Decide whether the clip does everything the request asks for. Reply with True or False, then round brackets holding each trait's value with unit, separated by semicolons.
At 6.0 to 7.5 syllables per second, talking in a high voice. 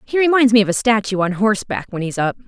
True (6.7 syllables/s; 215 Hz)